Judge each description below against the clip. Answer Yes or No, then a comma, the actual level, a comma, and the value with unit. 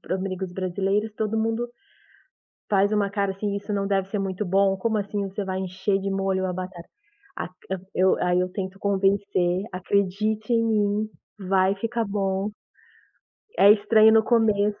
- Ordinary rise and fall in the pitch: No, narrow, 1.8 semitones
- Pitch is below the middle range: No, high, 200 Hz